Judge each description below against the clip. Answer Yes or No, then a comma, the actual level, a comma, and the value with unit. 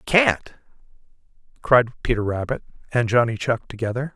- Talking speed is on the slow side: Yes, slow, 115 wpm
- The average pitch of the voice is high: No, low, 120 Hz